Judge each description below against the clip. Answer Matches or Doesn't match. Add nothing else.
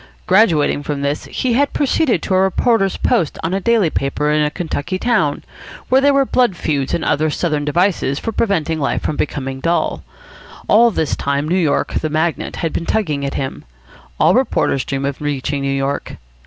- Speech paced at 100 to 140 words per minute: Doesn't match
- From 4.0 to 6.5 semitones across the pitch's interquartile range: Matches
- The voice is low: Doesn't match